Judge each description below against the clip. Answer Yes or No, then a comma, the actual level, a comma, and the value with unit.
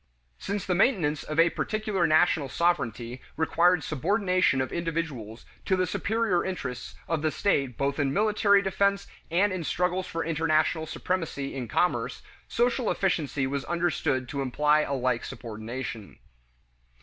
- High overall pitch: No, medium, 160 Hz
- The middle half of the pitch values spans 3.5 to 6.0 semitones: Yes, average, 5.3 semitones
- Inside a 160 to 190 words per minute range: No, average, 140 wpm